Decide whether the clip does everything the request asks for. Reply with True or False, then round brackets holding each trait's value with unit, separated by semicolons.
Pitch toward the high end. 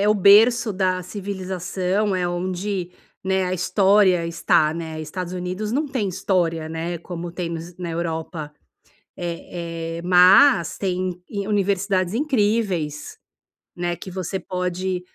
False (180 Hz)